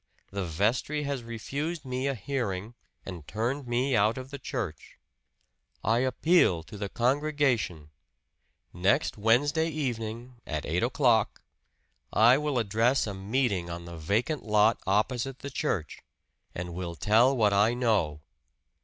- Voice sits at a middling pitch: No, low, 115 Hz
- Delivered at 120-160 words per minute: Yes, slow, 135 wpm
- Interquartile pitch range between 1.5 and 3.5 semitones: No, average, 5.1 semitones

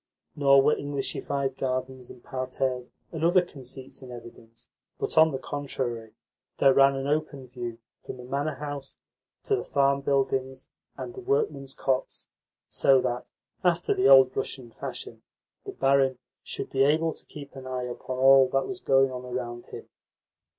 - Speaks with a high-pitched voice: No, low, 135 Hz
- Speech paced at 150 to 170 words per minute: Yes, average, 165 wpm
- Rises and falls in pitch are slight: Yes, narrow, 1.8 semitones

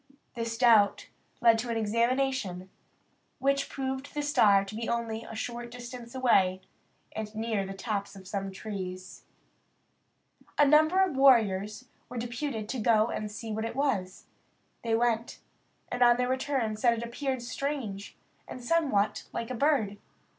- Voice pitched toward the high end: Yes, high, 235 Hz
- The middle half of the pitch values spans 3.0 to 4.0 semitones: Yes, average, 3.5 semitones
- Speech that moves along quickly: No, average, 155 wpm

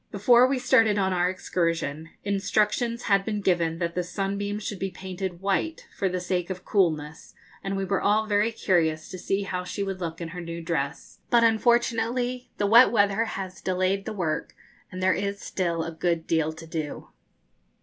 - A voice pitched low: No, high, 190 Hz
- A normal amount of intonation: Yes, average, 3.3 semitones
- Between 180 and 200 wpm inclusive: Yes, average, 190 wpm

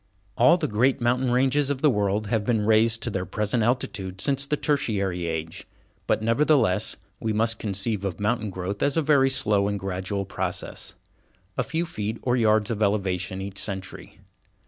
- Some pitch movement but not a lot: Yes, average, 4.3 semitones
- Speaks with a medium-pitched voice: No, low, 110 Hz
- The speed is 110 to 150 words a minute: No, average, 175 wpm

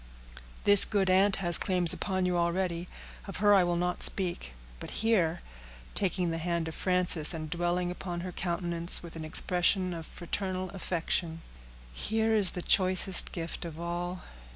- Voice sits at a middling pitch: Yes, medium, 180 Hz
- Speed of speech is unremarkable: Yes, average, 160 wpm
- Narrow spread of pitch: Yes, narrow, 1.6 semitones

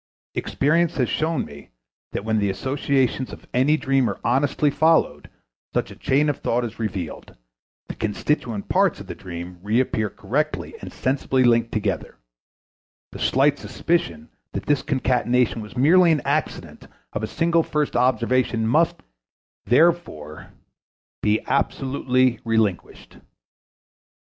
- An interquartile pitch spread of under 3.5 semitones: No, average, 5.0 semitones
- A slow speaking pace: Yes, slow, 130 wpm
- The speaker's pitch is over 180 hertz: No, low, 125 Hz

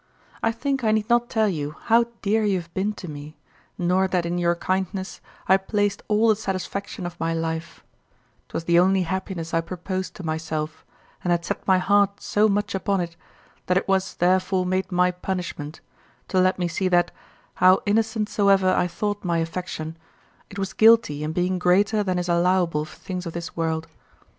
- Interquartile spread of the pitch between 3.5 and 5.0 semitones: No, average, 2.8 semitones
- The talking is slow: No, average, 190 wpm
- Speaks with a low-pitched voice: No, medium, 185 Hz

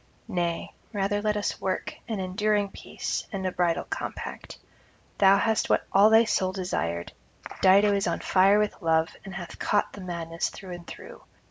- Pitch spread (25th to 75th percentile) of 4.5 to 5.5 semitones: No, narrow, 2.6 semitones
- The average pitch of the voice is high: Yes, high, 195 Hz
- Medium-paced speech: Yes, average, 170 wpm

